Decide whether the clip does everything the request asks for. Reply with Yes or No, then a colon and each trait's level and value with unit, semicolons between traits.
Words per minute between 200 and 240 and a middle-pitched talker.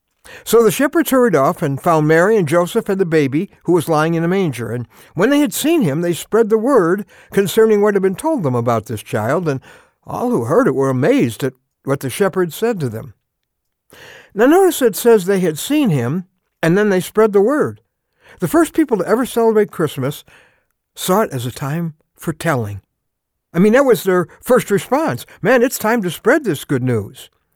Yes: fast, 205 wpm; medium, 175 Hz